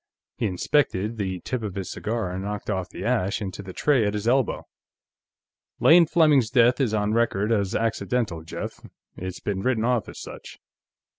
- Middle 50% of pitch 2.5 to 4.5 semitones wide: Yes, average, 4.2 semitones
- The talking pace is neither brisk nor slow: Yes, average, 175 wpm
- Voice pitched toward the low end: Yes, low, 110 Hz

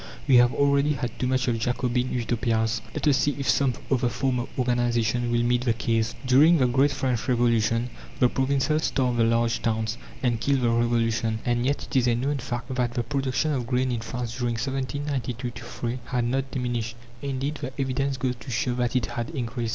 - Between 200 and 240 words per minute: Yes, fast, 205 wpm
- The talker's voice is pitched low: Yes, low, 125 Hz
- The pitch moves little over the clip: Yes, narrow, 2.0 semitones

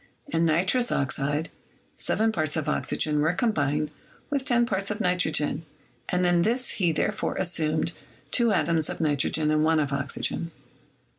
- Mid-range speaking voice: Yes, medium, 165 Hz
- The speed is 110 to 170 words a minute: Yes, average, 150 wpm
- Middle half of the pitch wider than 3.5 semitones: Yes, average, 4.5 semitones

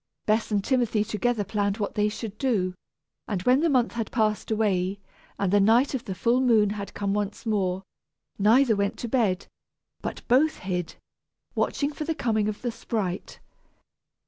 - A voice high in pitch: Yes, high, 215 Hz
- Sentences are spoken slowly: No, average, 170 wpm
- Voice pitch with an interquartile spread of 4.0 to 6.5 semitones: No, average, 3.3 semitones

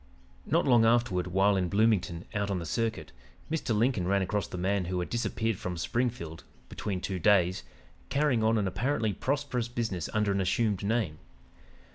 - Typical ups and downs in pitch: Yes, average, 4.2 semitones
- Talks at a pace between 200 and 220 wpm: No, average, 170 wpm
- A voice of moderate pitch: No, low, 105 Hz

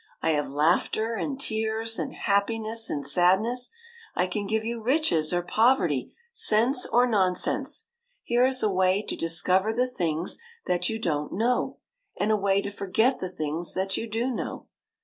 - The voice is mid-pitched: No, high, 210 Hz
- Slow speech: No, average, 170 wpm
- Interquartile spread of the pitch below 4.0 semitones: No, average, 4.4 semitones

